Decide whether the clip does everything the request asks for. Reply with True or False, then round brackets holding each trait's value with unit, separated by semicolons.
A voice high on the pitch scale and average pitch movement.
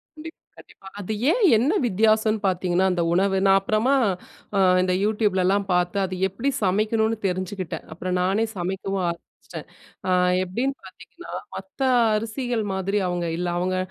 True (195 Hz; 3.2 semitones)